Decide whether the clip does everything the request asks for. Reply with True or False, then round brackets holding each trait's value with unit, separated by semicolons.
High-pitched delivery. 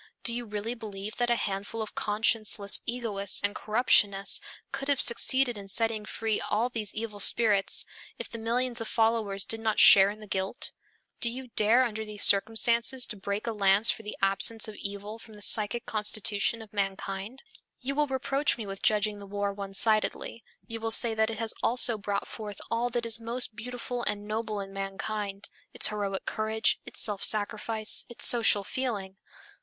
True (215 Hz)